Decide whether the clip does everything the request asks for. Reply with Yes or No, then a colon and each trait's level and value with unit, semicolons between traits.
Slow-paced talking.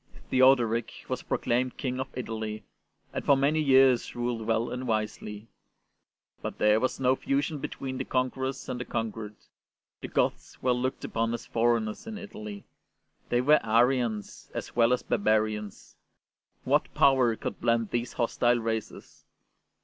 No: average, 145 wpm